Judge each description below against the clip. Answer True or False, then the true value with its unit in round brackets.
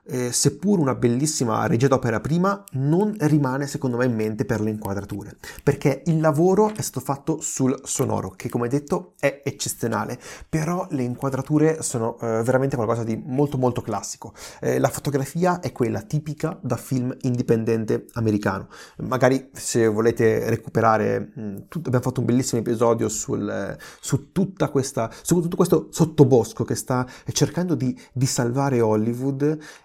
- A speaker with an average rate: True (155 wpm)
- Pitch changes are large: False (4.3 semitones)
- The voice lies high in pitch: False (130 Hz)